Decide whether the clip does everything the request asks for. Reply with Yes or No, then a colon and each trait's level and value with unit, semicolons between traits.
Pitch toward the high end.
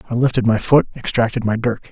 No: low, 120 Hz